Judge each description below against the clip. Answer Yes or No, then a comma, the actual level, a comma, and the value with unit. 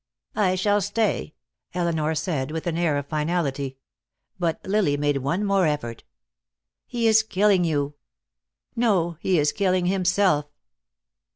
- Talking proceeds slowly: Yes, slow, 130 wpm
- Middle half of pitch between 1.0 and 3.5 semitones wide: No, average, 4.8 semitones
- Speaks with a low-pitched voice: No, medium, 175 Hz